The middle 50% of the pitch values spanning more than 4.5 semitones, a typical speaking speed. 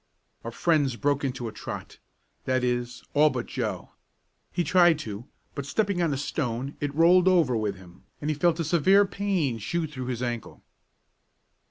Yes: wide, 5.6 semitones; average, 175 wpm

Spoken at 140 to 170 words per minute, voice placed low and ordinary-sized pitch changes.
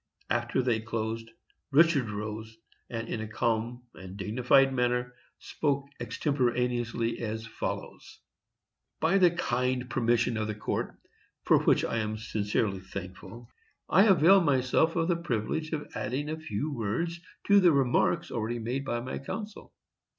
Yes: average, 145 wpm; low, 120 Hz; average, 4.6 semitones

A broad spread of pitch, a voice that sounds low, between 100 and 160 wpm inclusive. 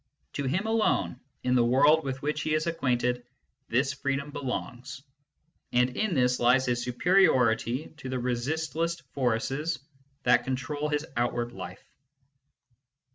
No: average, 3.5 semitones; low, 130 Hz; slow, 135 wpm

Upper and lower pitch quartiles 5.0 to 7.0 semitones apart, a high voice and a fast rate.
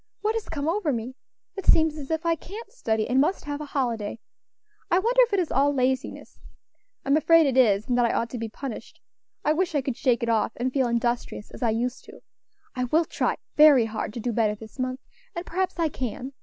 Yes: average, 5.3 semitones; very high, 265 Hz; fast, 230 wpm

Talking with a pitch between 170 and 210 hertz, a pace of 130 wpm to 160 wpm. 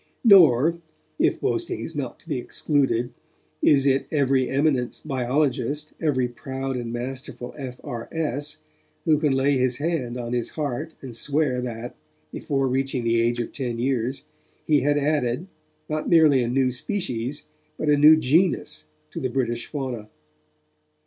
No: low, 135 Hz; average, 150 wpm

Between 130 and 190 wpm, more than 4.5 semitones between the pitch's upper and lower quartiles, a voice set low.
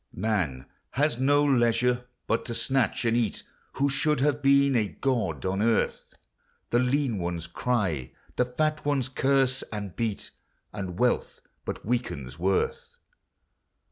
Yes: average, 140 wpm; average, 5.3 semitones; low, 120 Hz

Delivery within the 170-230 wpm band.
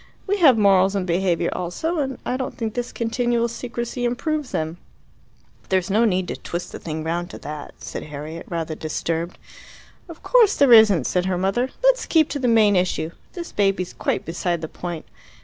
Yes: average, 185 wpm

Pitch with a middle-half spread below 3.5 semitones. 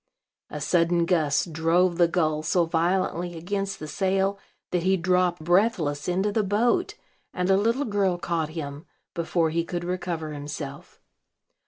Yes: average, 2.9 semitones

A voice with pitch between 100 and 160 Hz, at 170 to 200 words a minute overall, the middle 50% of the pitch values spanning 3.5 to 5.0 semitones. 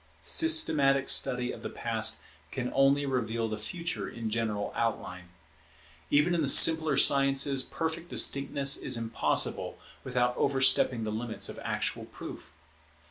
No: low, 135 Hz; slow, 135 wpm; average, 3.8 semitones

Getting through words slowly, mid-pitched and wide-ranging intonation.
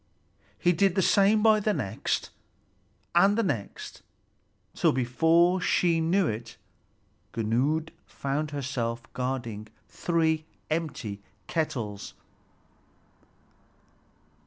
Yes: slow, 90 wpm; medium, 155 Hz; wide, 6.7 semitones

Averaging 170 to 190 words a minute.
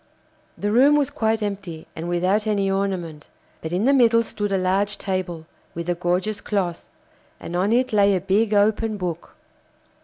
Yes: average, 175 wpm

